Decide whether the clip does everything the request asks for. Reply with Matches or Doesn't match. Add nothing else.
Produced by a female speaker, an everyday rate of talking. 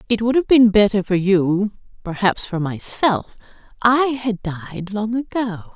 Matches